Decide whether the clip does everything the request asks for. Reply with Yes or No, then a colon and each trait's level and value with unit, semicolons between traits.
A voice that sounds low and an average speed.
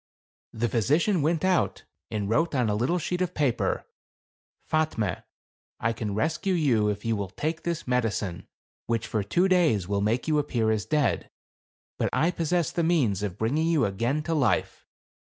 Yes: low, 125 Hz; average, 175 wpm